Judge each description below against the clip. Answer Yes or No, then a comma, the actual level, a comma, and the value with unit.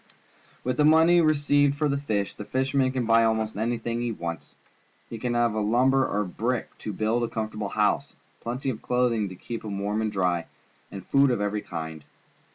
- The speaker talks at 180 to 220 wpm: Yes, average, 195 wpm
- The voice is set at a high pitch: No, low, 115 Hz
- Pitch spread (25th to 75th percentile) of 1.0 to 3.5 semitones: No, average, 3.9 semitones